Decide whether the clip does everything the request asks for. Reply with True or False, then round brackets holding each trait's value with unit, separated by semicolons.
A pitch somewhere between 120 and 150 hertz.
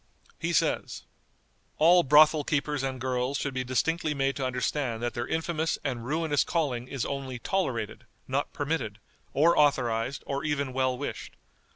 True (140 Hz)